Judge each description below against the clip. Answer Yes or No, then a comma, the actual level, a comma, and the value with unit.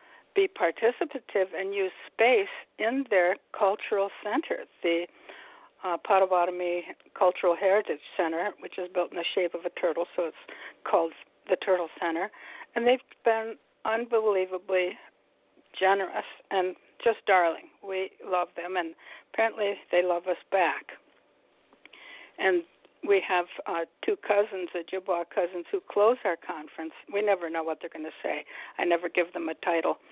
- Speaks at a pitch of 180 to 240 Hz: Yes, high, 190 Hz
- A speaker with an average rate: Yes, average, 145 wpm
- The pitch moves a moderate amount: Yes, average, 4.3 semitones